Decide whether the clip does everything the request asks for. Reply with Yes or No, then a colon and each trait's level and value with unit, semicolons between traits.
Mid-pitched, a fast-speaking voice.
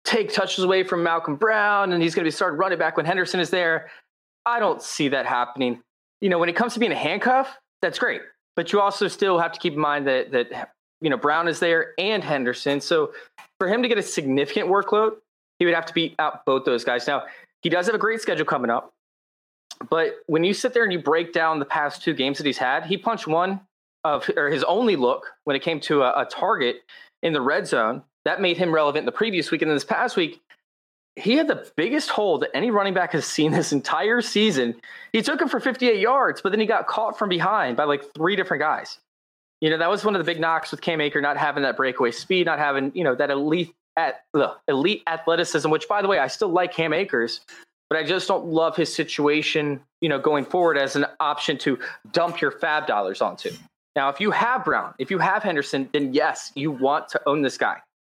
Yes: medium, 170 Hz; fast, 235 wpm